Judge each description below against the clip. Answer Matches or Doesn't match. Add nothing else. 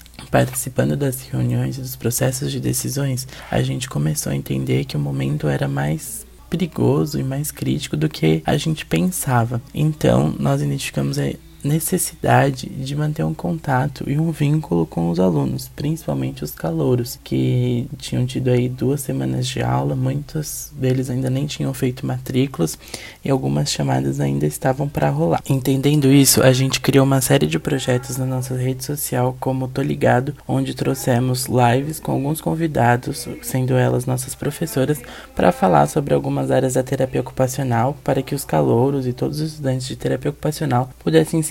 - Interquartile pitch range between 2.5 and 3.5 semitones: Doesn't match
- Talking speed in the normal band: Matches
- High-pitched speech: Doesn't match